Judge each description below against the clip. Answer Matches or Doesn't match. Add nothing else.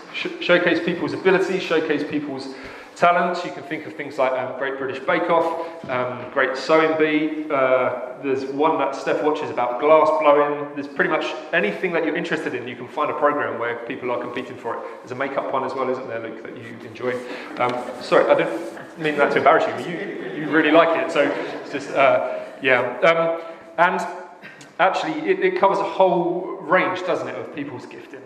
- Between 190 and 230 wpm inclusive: Matches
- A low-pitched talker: Doesn't match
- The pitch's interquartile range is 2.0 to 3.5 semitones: Doesn't match